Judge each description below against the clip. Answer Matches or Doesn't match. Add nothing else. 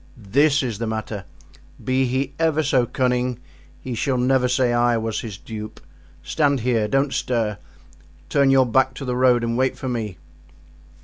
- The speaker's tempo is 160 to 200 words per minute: Matches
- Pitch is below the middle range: Matches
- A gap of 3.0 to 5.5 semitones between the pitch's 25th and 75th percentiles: Doesn't match